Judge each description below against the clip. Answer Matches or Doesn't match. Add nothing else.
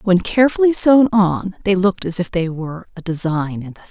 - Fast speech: Matches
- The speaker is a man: Doesn't match